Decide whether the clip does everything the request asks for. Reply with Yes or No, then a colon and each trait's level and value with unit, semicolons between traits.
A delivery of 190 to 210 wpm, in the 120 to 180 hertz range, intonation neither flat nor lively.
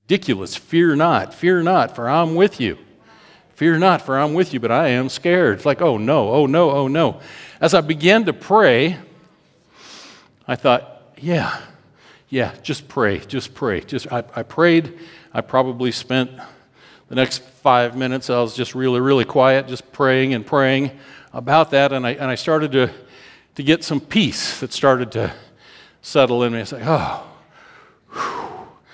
No: average, 175 wpm; low, 135 Hz; average, 4.5 semitones